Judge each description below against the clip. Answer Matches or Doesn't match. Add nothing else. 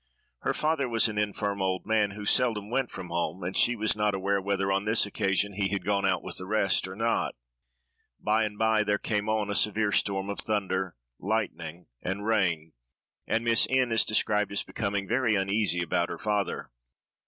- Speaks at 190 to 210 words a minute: Matches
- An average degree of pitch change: Doesn't match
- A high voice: Doesn't match